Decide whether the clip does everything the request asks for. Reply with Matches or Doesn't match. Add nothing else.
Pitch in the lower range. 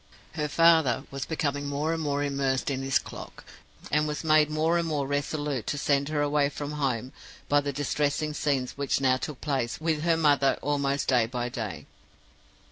Doesn't match